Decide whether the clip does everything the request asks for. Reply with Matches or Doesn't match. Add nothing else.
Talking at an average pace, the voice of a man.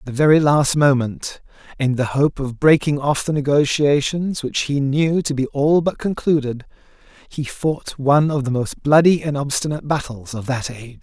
Matches